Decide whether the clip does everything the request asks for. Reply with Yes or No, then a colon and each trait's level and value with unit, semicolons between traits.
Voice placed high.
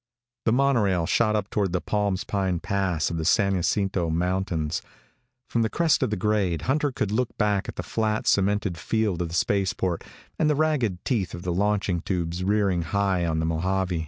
No: very low, 95 Hz